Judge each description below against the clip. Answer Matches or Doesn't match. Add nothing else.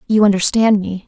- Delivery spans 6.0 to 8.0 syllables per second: Doesn't match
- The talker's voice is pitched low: Doesn't match